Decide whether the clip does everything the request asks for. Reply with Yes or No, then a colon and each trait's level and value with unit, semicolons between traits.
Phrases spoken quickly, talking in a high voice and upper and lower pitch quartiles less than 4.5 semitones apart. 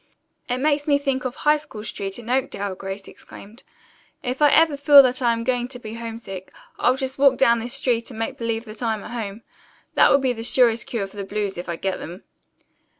Yes: fast, 220 wpm; high, 235 Hz; average, 3.7 semitones